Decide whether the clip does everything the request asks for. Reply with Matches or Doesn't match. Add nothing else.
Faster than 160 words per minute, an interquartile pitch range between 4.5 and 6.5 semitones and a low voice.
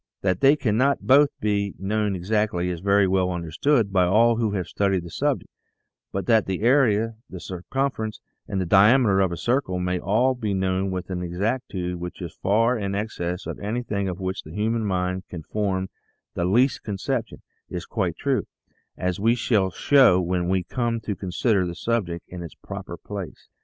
Doesn't match